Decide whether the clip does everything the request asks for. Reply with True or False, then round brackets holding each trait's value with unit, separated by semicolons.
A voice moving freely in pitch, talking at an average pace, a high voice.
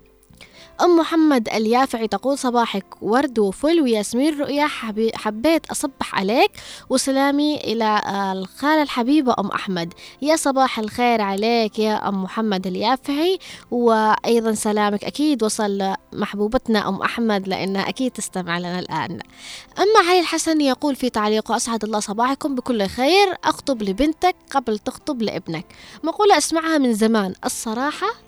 True (5.9 semitones; 125 wpm; 235 Hz)